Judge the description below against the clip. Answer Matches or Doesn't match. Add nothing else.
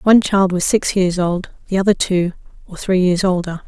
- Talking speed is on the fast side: Matches